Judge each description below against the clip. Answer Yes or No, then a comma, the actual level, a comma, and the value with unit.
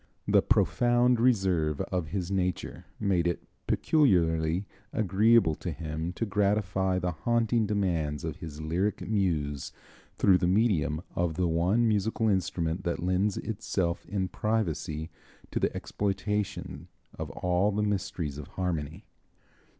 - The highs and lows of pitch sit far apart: No, average, 4.0 semitones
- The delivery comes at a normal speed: No, slow, 130 wpm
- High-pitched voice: No, very low, 90 Hz